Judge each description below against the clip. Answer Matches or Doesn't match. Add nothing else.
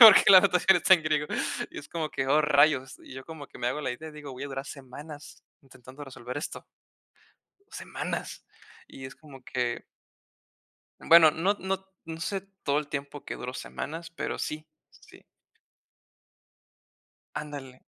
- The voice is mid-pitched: Matches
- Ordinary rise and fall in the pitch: Matches